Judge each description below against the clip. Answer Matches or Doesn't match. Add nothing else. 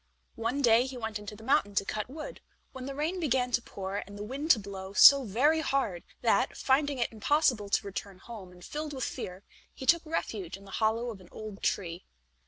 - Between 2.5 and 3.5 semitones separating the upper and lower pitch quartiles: Doesn't match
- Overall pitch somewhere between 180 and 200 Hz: Doesn't match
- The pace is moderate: Doesn't match